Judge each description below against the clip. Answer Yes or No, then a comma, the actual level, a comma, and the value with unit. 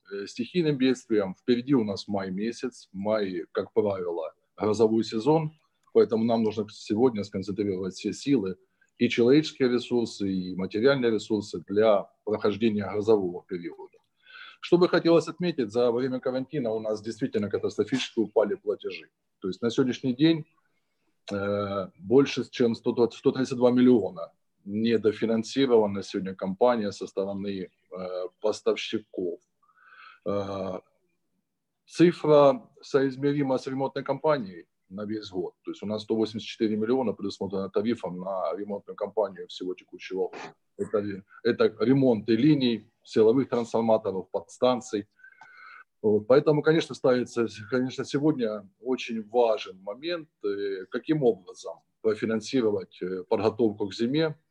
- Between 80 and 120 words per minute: Yes, average, 110 wpm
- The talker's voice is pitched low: Yes, low, 120 Hz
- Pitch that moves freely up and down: Yes, wide, 6.4 semitones